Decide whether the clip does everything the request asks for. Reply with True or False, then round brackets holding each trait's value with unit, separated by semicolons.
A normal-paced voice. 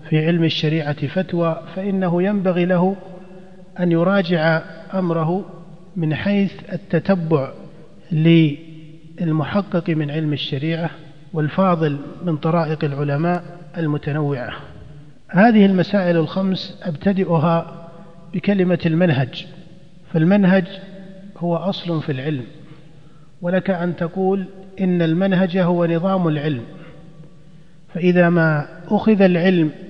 True (90 wpm)